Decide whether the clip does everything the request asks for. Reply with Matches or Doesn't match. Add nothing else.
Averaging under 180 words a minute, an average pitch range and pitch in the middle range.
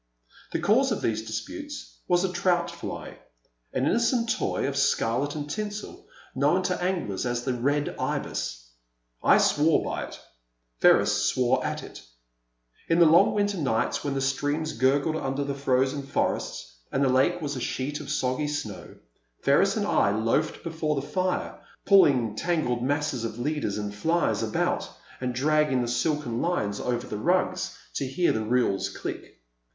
Doesn't match